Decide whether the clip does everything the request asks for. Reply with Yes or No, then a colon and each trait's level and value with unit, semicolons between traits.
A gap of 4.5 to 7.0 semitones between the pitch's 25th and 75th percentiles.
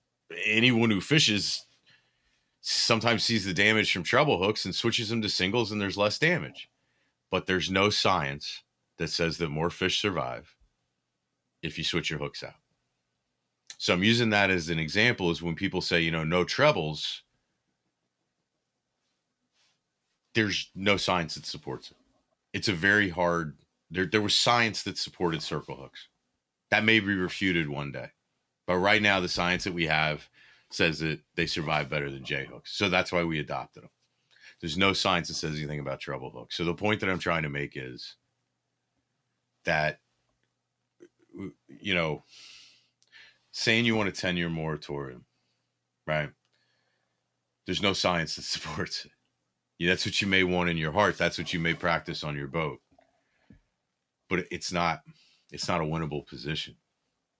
Yes: average, 5.3 semitones